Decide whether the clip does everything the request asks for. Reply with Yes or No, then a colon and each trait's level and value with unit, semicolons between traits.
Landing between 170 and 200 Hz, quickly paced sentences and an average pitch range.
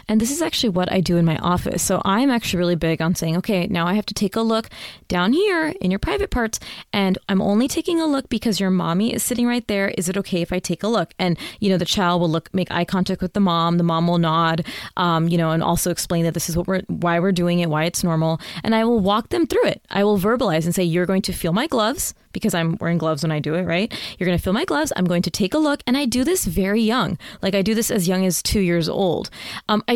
Yes: medium, 185 Hz; fast, 290 wpm; average, 4.3 semitones